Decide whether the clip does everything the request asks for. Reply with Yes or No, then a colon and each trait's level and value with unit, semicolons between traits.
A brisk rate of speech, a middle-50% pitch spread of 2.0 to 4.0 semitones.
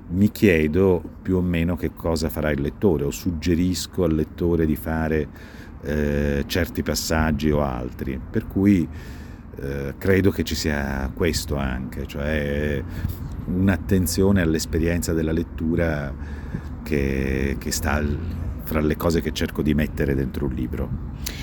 No: average, 135 wpm; average, 2.8 semitones